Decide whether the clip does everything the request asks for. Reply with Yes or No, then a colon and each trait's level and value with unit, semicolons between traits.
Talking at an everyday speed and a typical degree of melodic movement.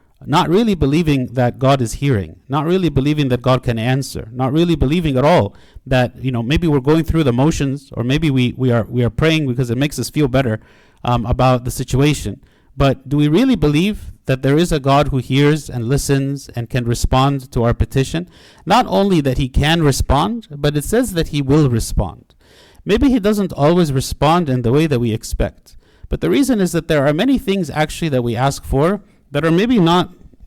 No: fast, 215 wpm; average, 4.3 semitones